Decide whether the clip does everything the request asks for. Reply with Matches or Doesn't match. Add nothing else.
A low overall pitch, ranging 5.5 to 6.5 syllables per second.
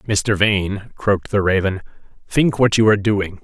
Doesn't match